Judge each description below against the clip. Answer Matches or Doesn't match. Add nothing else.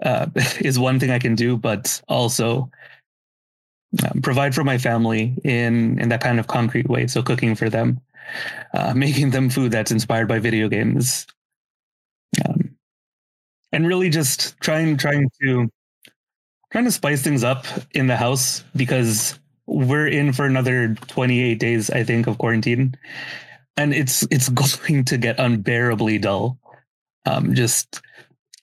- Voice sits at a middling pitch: Doesn't match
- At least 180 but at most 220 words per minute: Doesn't match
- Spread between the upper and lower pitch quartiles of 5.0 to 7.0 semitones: Doesn't match